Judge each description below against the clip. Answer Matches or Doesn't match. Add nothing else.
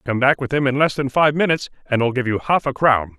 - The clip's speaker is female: Doesn't match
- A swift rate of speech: Matches